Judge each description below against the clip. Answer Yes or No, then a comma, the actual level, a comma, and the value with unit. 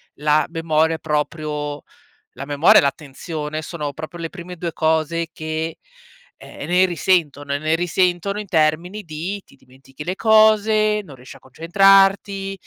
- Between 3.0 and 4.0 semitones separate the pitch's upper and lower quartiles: Yes, average, 3.6 semitones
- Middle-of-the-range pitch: Yes, medium, 165 Hz